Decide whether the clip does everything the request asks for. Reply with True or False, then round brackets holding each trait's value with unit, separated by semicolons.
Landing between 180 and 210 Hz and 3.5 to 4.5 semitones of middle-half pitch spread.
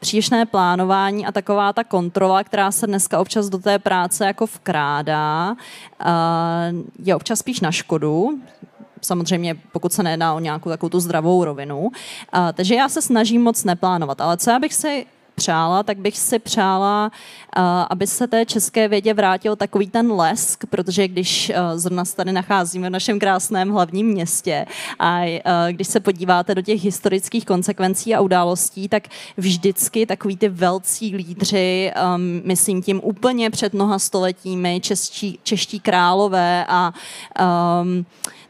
False (190 Hz; 2.8 semitones)